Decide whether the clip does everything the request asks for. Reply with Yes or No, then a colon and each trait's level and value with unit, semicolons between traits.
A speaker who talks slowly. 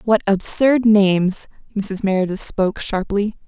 Yes: slow, 120 wpm